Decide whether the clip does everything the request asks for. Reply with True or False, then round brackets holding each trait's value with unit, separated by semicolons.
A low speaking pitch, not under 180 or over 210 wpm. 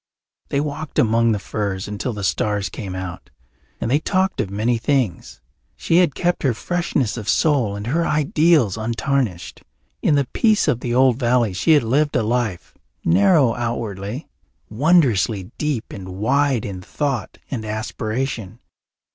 False (120 Hz; 155 wpm)